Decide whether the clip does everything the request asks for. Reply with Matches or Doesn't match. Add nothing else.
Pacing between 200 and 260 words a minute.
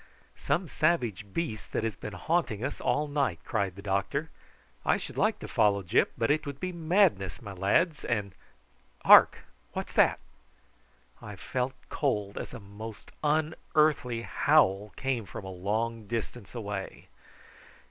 Doesn't match